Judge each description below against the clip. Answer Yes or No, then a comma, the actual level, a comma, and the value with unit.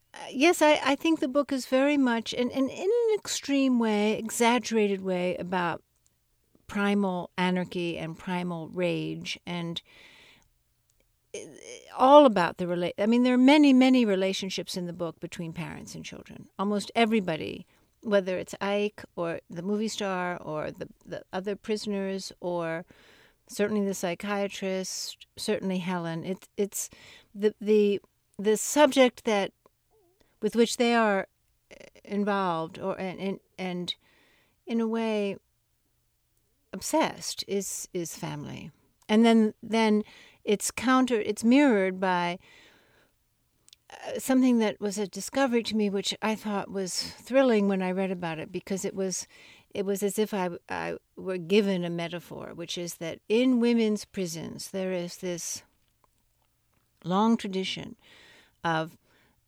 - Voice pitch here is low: No, high, 200 Hz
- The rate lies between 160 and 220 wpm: No, slow, 135 wpm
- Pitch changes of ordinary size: Yes, average, 3.9 semitones